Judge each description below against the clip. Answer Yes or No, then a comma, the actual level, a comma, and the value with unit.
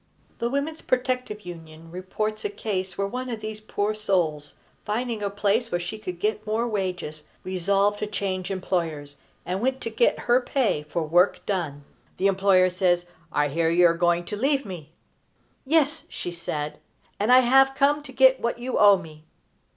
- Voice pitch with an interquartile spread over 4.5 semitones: Yes, average, 5.3 semitones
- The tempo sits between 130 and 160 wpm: No, average, 180 wpm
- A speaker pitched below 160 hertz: No, high, 200 Hz